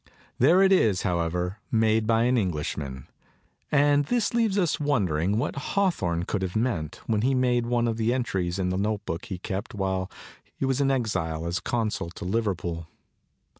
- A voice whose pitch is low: Yes, low, 110 Hz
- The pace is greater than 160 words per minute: Yes, average, 170 wpm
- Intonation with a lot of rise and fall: Yes, wide, 6.1 semitones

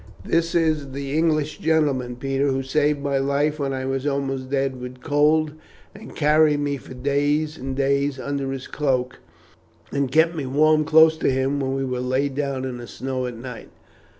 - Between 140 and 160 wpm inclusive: No, average, 180 wpm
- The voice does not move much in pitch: Yes, narrow, 2.2 semitones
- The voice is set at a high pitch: No, medium, 140 Hz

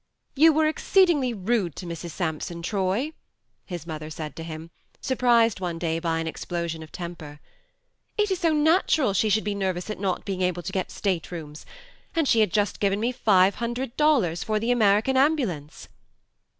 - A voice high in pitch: Yes, high, 195 Hz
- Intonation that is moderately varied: No, wide, 6.4 semitones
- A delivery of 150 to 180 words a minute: No, average, 190 wpm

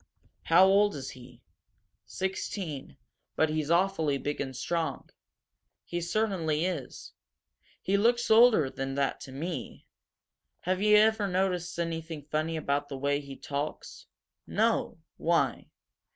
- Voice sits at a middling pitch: Yes, medium, 165 Hz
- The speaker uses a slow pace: Yes, slow, 125 wpm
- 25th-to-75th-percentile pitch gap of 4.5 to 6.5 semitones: Yes, average, 5.0 semitones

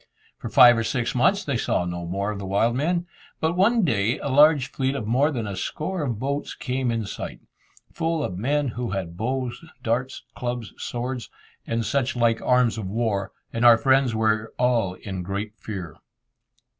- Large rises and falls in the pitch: No, average, 4.1 semitones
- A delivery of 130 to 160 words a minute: No, average, 185 wpm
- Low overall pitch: Yes, low, 120 Hz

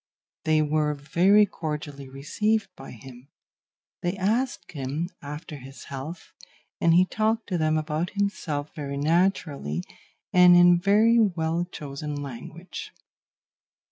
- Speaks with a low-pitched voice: No, medium, 160 Hz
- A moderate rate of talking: No, slow, 120 wpm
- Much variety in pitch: No, average, 4.4 semitones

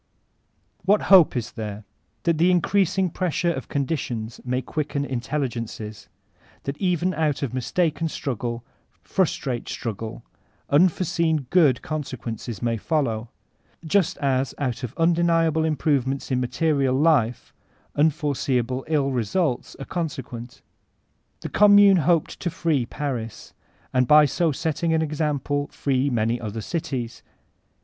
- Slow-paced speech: Yes, slow, 125 wpm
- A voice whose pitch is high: No, medium, 145 Hz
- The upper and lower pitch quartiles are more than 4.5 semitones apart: Yes, average, 4.9 semitones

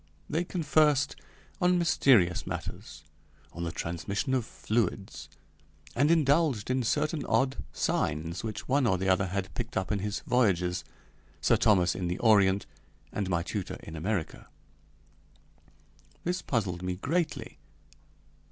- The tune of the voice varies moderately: No, wide, 7.2 semitones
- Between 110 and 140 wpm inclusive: Yes, slow, 135 wpm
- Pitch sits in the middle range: No, low, 105 Hz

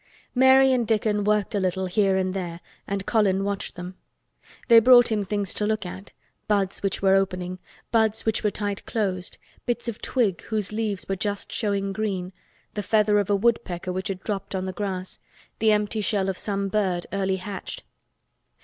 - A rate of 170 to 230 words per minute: Yes, average, 180 wpm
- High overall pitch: Yes, high, 200 Hz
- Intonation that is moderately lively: No, narrow, 2.2 semitones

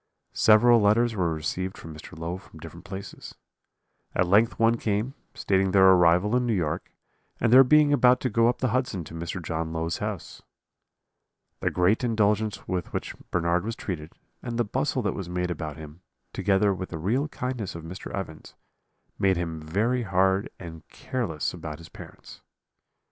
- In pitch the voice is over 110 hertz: No, very low, 95 Hz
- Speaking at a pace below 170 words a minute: No, average, 175 wpm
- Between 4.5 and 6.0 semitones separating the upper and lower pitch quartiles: Yes, average, 5.2 semitones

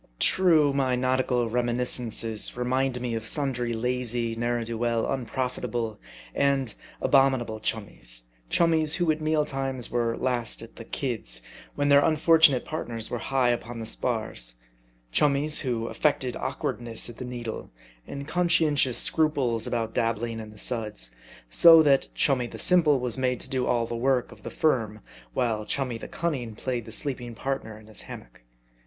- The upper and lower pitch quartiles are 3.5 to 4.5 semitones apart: No, average, 3.1 semitones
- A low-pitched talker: Yes, low, 125 Hz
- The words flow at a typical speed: Yes, average, 160 wpm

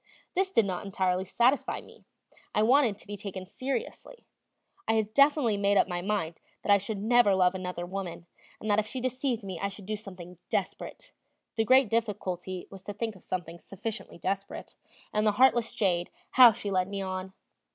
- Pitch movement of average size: Yes, average, 3.4 semitones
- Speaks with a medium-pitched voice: No, high, 200 Hz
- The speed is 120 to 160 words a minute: No, average, 190 wpm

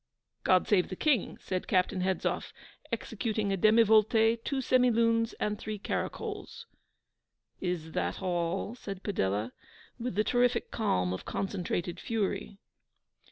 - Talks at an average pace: No, slow, 120 wpm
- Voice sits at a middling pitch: No, high, 205 Hz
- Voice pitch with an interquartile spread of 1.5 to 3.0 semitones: No, average, 3.9 semitones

